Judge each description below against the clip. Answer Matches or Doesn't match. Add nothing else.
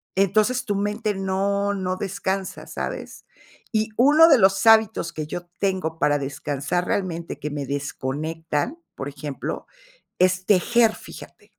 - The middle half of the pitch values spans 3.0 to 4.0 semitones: Doesn't match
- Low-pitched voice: Doesn't match